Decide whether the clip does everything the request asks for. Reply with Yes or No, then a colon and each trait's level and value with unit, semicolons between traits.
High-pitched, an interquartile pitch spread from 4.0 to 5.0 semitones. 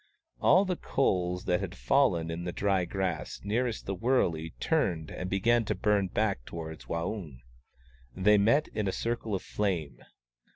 No: very low, 95 Hz; average, 4.4 semitones